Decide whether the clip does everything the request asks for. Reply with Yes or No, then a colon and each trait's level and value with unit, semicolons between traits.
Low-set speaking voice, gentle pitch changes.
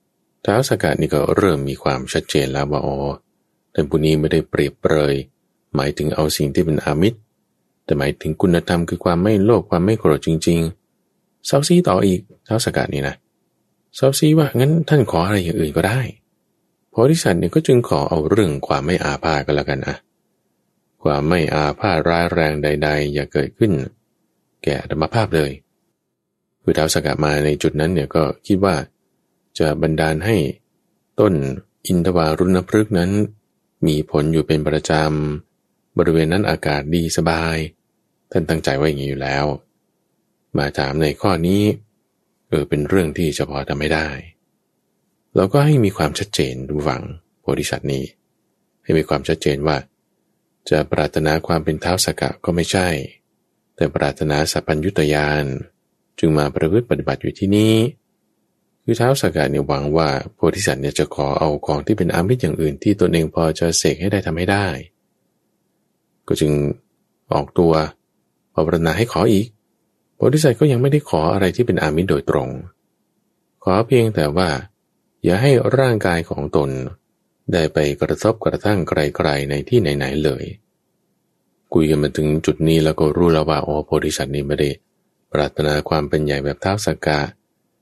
No: very low, 80 Hz; average, 4.0 semitones